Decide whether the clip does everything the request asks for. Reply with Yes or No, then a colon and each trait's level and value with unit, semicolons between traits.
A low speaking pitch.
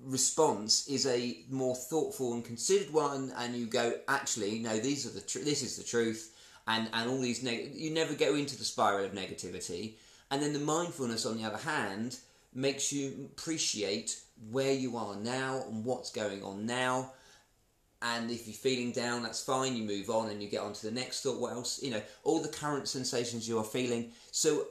Yes: low, 125 Hz